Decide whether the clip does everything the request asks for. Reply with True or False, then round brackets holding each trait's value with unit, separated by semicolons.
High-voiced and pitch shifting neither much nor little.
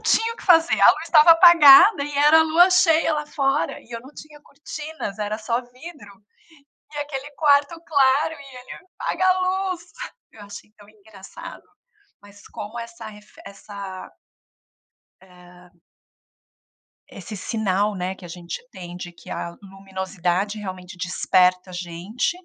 False (225 Hz; 7.9 semitones)